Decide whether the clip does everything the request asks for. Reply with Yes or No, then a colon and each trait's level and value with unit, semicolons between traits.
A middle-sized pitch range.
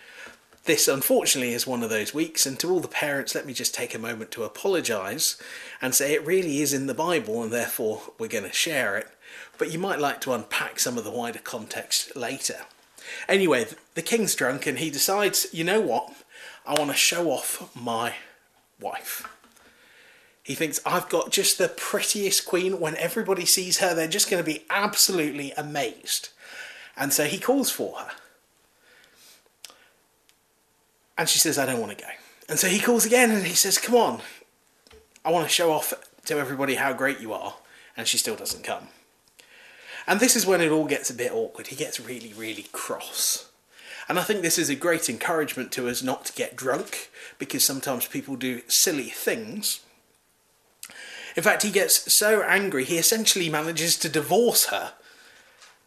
No: wide, 7.1 semitones